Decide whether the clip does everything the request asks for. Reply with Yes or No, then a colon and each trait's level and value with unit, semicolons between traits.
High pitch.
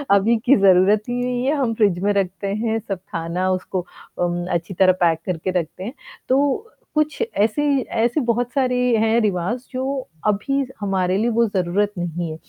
Yes: high, 205 Hz